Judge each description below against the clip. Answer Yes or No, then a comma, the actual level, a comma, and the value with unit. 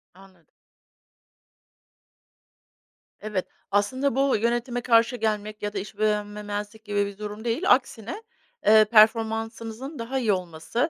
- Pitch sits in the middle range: No, high, 215 Hz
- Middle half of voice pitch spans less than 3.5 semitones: Yes, narrow, 2.4 semitones